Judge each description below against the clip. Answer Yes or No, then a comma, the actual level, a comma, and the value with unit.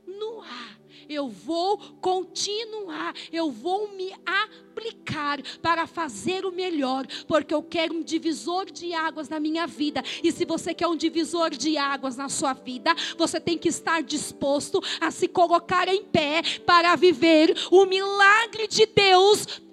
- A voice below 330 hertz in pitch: No, very high, 335 Hz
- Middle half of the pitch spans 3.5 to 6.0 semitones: No, average, 3.0 semitones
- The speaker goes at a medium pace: Yes, average, 150 wpm